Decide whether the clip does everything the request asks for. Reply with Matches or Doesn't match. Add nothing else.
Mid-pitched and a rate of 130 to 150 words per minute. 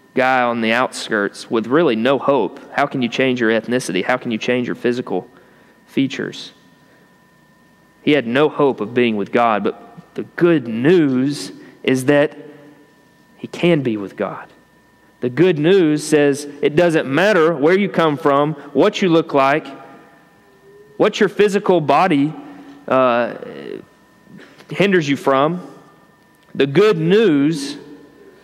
Matches